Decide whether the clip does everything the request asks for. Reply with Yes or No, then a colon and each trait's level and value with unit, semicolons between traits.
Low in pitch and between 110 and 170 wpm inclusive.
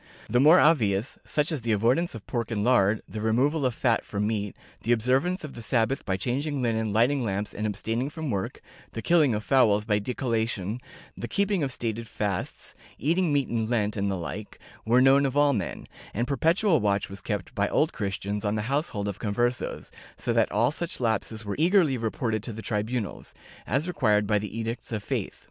No: low, 115 Hz; average, 200 wpm